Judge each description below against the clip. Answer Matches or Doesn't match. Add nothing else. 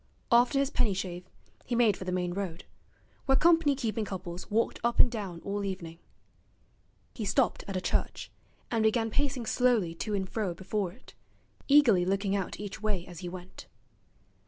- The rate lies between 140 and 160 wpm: Doesn't match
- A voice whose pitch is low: Doesn't match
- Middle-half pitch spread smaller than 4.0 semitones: Doesn't match